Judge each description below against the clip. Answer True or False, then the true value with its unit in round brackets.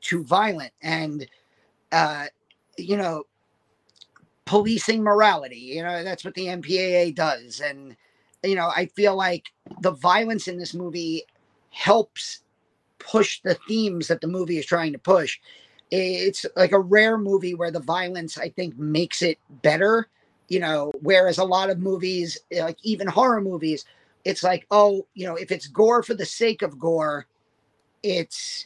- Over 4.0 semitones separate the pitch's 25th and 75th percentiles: False (3.2 semitones)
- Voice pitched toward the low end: False (180 Hz)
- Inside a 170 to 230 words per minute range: False (155 wpm)